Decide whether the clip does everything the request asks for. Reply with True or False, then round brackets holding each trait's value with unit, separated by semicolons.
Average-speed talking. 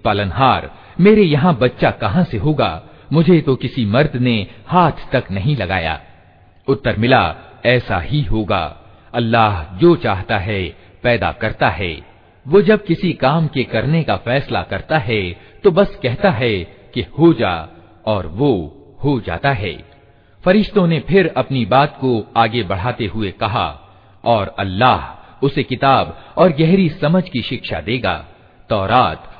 True (145 wpm)